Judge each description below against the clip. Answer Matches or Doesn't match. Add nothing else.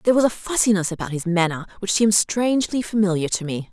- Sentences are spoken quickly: Matches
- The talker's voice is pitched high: Matches